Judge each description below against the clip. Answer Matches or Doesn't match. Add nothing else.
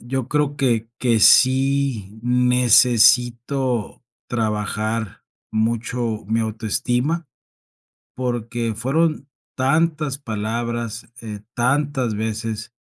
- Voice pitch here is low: Matches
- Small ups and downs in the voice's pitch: Doesn't match